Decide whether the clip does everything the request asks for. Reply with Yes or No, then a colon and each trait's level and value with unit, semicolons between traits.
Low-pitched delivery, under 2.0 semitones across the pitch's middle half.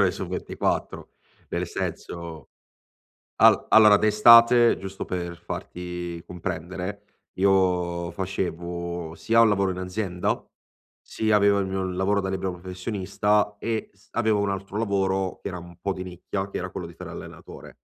No: very low, 95 Hz; narrow, 2.5 semitones